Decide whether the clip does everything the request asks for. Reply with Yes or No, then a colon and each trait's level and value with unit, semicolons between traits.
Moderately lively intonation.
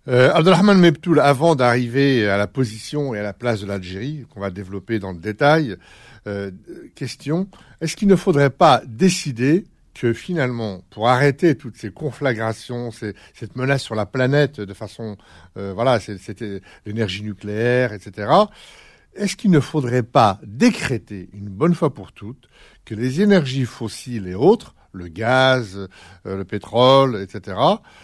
No: wide, 5.7 semitones